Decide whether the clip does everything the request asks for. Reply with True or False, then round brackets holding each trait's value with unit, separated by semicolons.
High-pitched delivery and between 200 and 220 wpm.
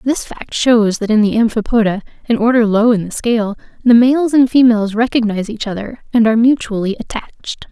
False (225 Hz; 185 wpm)